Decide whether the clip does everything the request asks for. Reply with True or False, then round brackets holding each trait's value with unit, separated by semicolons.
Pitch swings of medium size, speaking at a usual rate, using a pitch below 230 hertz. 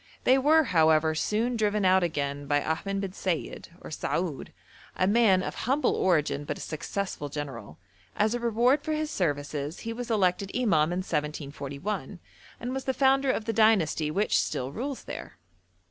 False (7.4 semitones; 170 wpm; 190 Hz)